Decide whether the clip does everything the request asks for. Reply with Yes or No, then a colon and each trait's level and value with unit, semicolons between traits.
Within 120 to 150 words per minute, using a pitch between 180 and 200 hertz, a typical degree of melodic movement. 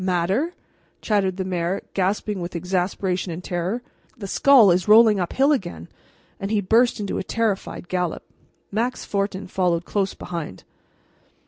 Yes: average, 145 wpm; high, 190 Hz; average, 3.0 semitones